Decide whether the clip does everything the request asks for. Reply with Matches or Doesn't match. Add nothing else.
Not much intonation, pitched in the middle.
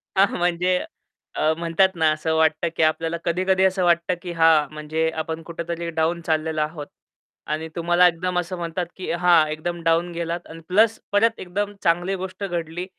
Matches